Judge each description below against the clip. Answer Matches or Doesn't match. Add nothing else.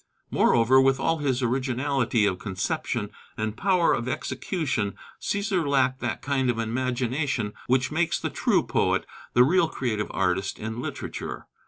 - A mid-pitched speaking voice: Doesn't match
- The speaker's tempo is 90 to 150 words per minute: Matches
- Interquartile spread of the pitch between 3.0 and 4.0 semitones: Matches